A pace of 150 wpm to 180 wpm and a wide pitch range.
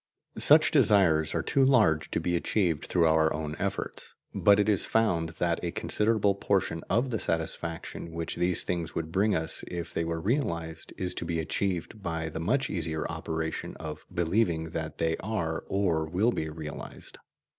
No: average, 175 wpm; average, 3.7 semitones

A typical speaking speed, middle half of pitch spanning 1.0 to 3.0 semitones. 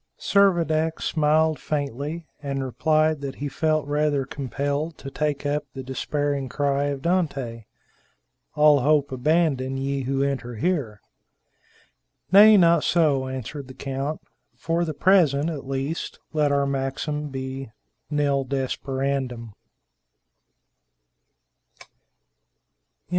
No: slow, 110 wpm; narrow, 2.4 semitones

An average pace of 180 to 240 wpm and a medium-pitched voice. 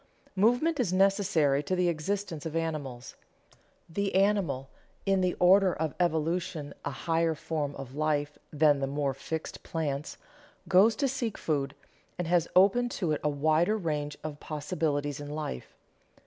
No: average, 150 wpm; medium, 160 Hz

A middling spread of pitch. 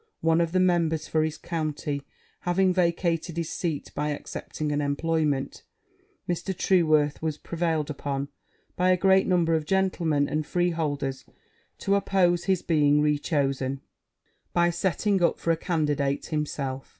Yes: average, 3.1 semitones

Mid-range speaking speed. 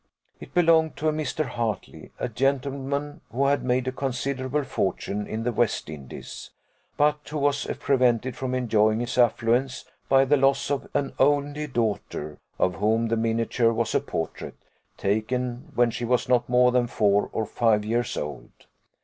Yes: average, 165 wpm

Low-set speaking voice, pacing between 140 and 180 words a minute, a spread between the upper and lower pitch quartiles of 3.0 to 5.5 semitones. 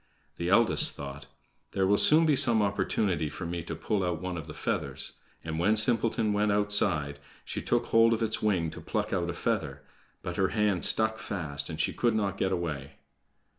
No: very low, 95 Hz; average, 200 wpm; average, 4.7 semitones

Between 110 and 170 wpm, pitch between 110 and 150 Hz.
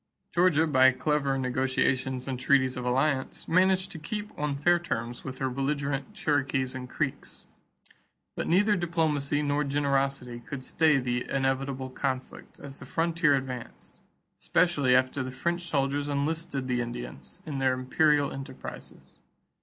Yes: average, 140 wpm; medium, 140 Hz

